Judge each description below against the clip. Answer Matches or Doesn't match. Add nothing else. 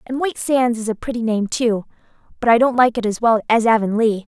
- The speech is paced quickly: Matches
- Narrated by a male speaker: Doesn't match